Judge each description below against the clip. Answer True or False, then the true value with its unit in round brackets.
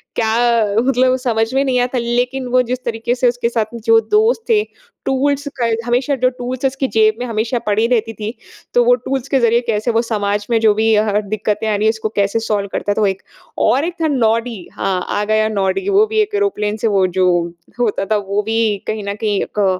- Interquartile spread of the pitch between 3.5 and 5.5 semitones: False (3.1 semitones)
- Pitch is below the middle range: False (230 Hz)